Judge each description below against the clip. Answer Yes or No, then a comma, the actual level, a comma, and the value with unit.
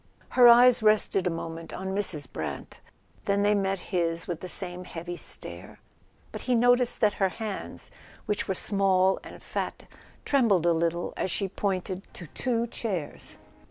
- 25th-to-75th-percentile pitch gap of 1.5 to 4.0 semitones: Yes, average, 3.4 semitones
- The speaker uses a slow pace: No, average, 160 wpm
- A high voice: Yes, high, 195 Hz